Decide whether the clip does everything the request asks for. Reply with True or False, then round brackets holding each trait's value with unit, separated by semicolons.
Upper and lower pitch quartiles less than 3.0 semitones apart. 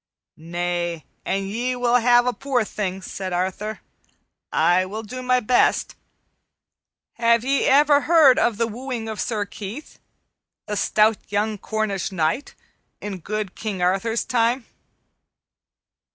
False (4.2 semitones)